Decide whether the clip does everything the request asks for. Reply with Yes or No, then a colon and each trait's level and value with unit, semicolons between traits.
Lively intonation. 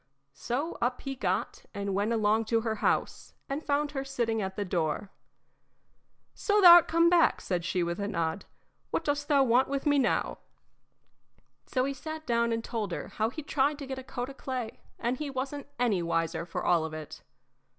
Yes: wide, 5.7 semitones